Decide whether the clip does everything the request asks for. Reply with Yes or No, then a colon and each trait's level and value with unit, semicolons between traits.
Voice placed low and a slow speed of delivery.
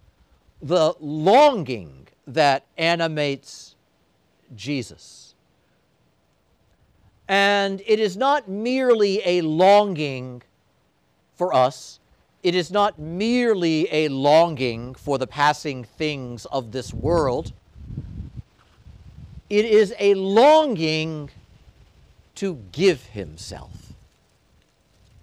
No: medium, 145 Hz; slow, 80 wpm